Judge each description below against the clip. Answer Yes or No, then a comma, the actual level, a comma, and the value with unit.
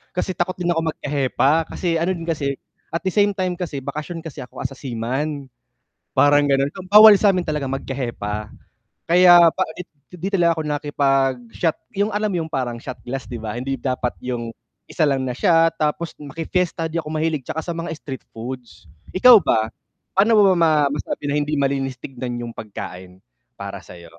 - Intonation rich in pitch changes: No, average, 4.9 semitones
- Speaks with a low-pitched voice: No, medium, 145 Hz